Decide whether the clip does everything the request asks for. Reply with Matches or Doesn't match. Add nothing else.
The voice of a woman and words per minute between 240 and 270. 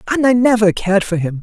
Doesn't match